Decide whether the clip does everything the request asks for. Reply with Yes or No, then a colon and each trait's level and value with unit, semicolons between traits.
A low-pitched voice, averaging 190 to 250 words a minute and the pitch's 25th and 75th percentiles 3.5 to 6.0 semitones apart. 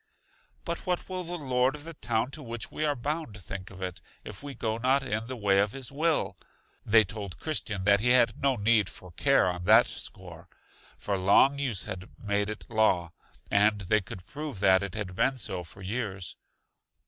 Yes: low, 110 Hz; average, 200 wpm; wide, 5.5 semitones